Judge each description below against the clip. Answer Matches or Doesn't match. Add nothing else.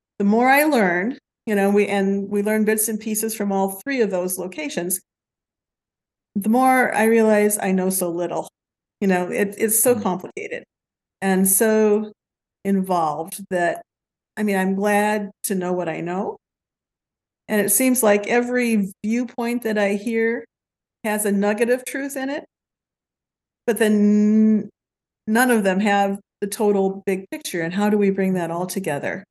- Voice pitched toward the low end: Doesn't match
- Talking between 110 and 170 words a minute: Matches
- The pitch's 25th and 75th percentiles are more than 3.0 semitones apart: Doesn't match